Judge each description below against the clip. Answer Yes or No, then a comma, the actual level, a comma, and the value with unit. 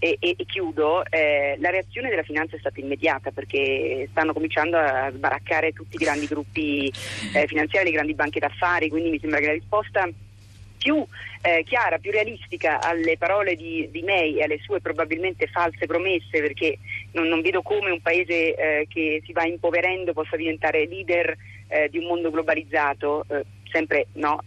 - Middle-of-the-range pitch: Yes, medium, 160 Hz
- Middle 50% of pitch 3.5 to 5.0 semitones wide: No, narrow, 2.6 semitones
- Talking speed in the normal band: No, fast, 175 wpm